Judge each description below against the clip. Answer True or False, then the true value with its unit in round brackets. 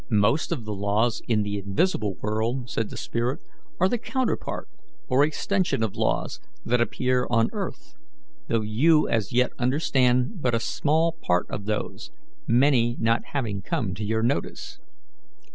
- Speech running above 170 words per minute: False (155 wpm)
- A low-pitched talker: True (120 Hz)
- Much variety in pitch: False (4.3 semitones)